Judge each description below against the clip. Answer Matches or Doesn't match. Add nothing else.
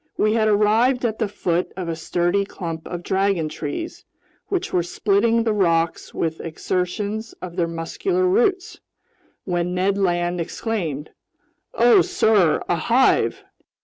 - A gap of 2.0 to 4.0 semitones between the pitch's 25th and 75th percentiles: Doesn't match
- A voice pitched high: Matches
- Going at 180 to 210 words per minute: Doesn't match